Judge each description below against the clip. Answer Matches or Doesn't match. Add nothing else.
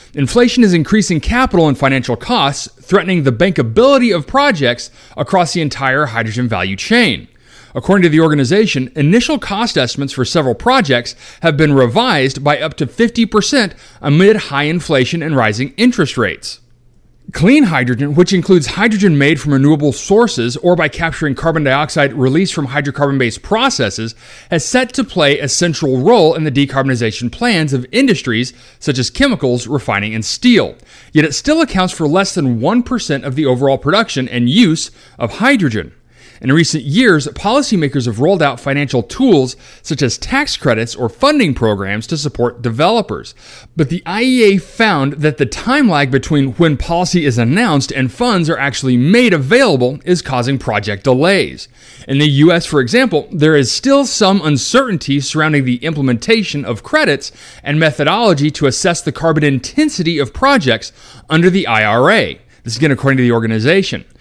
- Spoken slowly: Doesn't match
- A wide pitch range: Matches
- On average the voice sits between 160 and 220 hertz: Doesn't match